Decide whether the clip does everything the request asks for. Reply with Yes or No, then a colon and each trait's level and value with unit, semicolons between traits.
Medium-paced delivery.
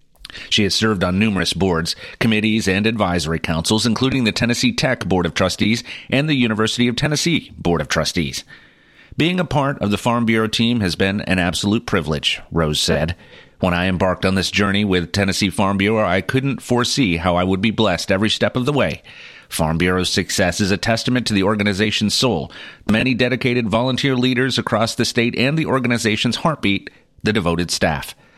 Yes: average, 185 wpm